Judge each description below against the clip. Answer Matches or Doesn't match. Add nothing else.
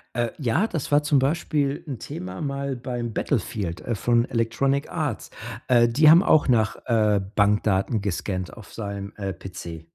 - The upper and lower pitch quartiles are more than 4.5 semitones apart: Matches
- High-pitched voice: Doesn't match